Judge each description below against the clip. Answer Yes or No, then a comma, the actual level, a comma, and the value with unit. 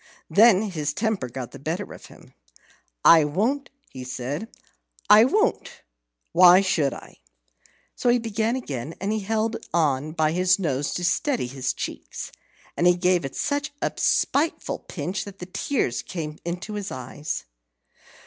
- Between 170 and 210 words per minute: No, average, 150 wpm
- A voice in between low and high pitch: Yes, medium, 180 Hz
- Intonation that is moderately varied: No, wide, 6.7 semitones